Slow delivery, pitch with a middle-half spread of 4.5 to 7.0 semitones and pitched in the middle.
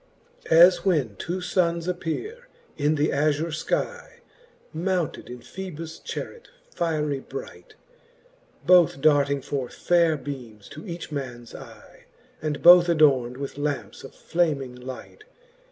No: slow, 125 wpm; average, 4.1 semitones; medium, 155 Hz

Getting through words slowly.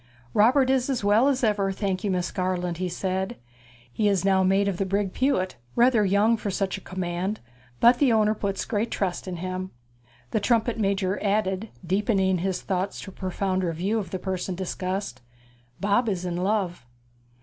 No: average, 185 wpm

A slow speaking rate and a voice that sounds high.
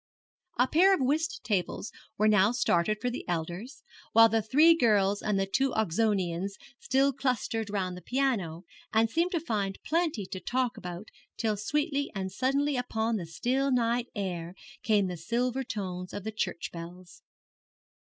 No: average, 165 wpm; high, 220 Hz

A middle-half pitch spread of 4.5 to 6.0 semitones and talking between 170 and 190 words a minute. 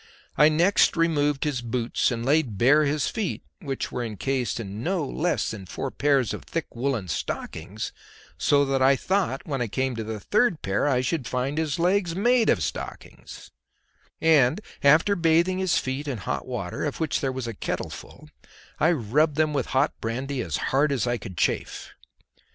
Yes: average, 4.8 semitones; average, 180 wpm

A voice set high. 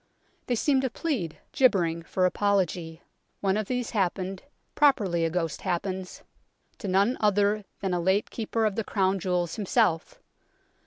Yes: high, 195 Hz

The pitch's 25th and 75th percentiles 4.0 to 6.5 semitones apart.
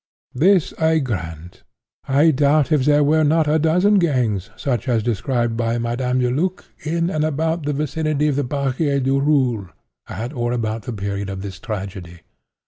Yes: average, 5.1 semitones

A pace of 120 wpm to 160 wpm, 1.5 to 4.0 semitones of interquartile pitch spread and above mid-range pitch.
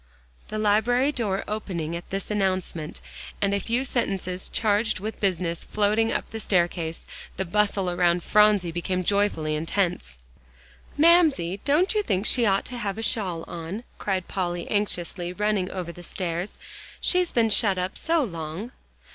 Yes: average, 155 wpm; average, 3.6 semitones; high, 195 Hz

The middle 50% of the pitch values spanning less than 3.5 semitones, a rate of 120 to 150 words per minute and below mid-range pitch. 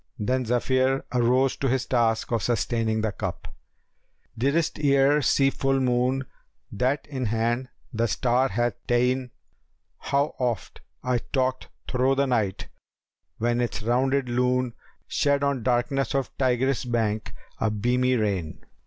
Yes: narrow, 2.4 semitones; average, 140 wpm; low, 125 Hz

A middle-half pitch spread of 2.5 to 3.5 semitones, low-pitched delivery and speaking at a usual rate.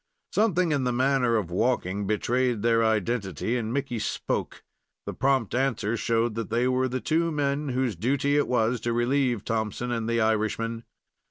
Yes: average, 2.9 semitones; low, 120 Hz; average, 170 wpm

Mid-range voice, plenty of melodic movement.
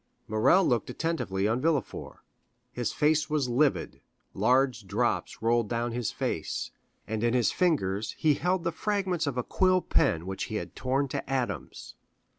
No: low, 125 Hz; wide, 5.9 semitones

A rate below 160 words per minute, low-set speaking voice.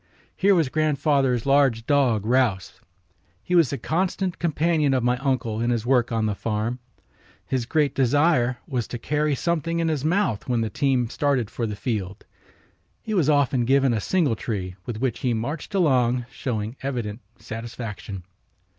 No: average, 165 wpm; low, 130 Hz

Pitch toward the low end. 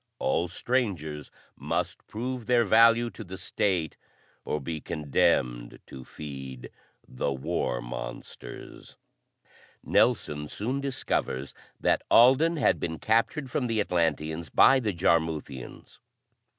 Yes: very low, 85 Hz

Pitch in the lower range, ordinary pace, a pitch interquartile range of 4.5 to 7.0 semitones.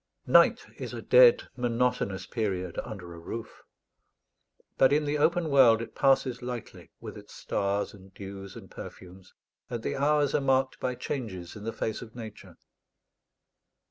Yes: low, 115 Hz; average, 155 wpm; average, 5.3 semitones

